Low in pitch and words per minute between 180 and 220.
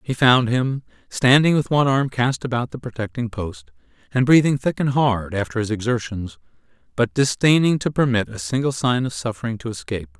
Yes: low, 120 Hz; average, 185 wpm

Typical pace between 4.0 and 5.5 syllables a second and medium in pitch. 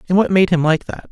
No: 6.5 syllables/s; medium, 165 Hz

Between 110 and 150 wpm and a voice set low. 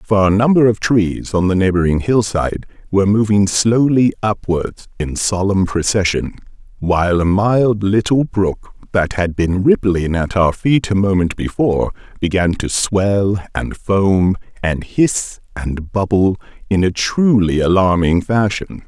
Yes: average, 145 wpm; low, 100 Hz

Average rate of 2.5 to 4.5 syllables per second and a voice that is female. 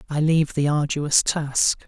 No: 4.3 syllables/s; male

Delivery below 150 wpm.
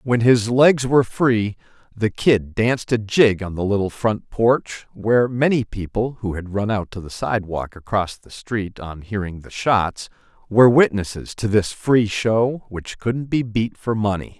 No: average, 185 wpm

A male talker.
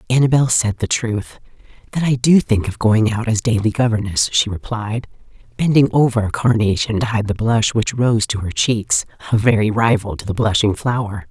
No: female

